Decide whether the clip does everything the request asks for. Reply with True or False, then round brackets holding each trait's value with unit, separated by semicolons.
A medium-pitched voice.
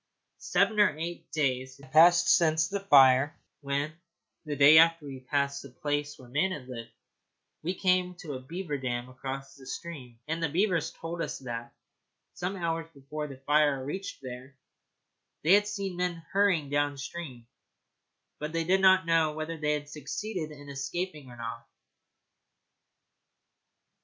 True (150 Hz)